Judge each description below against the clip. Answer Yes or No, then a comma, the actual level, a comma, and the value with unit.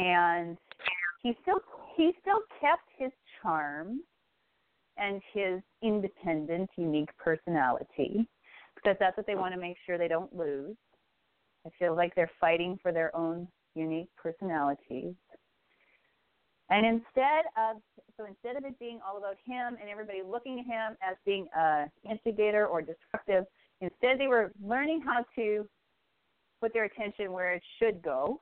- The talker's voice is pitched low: No, high, 200 Hz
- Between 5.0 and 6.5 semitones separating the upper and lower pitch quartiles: Yes, average, 5.3 semitones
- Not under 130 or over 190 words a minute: Yes, average, 145 wpm